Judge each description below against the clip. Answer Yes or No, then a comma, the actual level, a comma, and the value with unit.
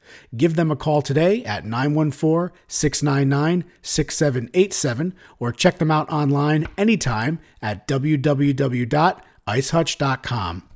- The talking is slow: Yes, slow, 95 wpm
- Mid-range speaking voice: Yes, medium, 150 Hz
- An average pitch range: Yes, average, 3.3 semitones